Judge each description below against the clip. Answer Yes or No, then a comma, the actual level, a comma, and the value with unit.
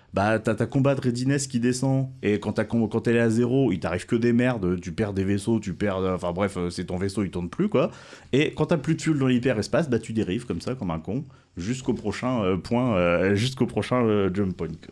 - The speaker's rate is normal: No, fast, 245 wpm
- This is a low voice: Yes, low, 110 Hz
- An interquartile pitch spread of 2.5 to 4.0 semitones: No, average, 4.9 semitones